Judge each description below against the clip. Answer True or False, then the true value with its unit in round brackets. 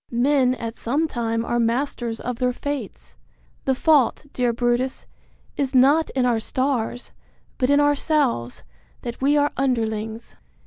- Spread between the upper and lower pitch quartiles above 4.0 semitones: False (3.4 semitones)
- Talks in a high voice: True (250 Hz)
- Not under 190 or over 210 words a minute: False (140 wpm)